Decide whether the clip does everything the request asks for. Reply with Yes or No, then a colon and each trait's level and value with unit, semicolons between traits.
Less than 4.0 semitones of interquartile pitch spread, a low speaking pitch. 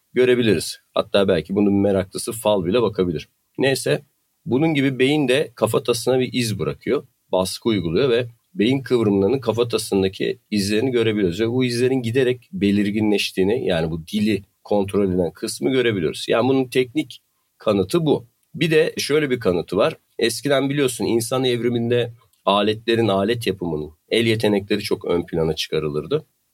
No: average, 4.3 semitones; low, 115 Hz